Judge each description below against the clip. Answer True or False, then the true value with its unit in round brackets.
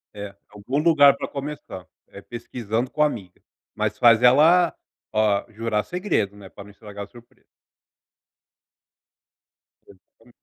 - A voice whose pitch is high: False (115 Hz)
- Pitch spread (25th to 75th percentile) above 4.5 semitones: True (5.6 semitones)